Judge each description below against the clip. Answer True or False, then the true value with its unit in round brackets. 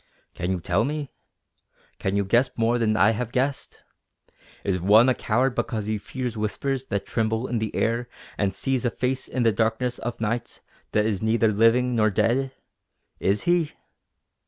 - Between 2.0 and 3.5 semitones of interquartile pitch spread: True (2.8 semitones)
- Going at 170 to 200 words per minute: True (175 wpm)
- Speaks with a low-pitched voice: True (115 Hz)